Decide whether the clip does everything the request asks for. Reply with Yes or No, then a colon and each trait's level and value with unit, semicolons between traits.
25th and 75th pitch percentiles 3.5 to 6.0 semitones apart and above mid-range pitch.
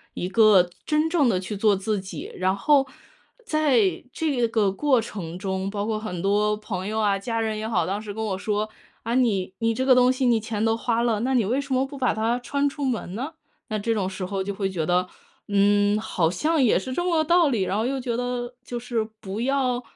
Yes: average, 4.2 semitones; high, 220 Hz